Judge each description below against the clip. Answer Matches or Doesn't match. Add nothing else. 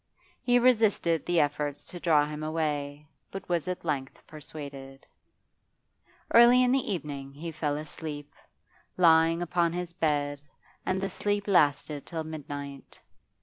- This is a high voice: Doesn't match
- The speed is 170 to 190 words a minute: Doesn't match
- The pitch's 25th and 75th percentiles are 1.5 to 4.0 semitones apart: Matches